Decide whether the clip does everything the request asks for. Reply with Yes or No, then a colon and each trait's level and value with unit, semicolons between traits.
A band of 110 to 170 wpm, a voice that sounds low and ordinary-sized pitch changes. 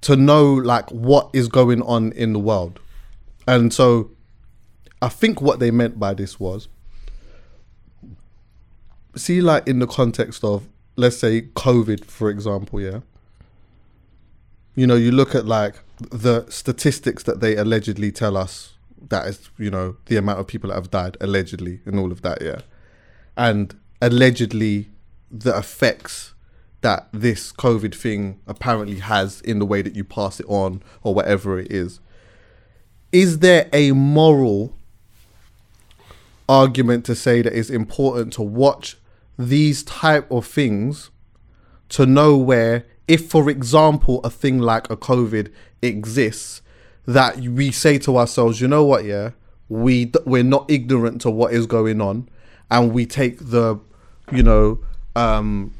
Yes: average, 150 wpm; low, 110 Hz; average, 3.5 semitones